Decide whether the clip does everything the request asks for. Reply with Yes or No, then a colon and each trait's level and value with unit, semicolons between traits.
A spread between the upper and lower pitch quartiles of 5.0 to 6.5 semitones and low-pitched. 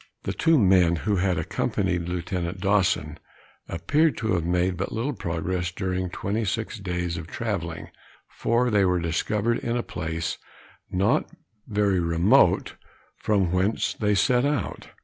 No: average, 3.7 semitones; very low, 95 Hz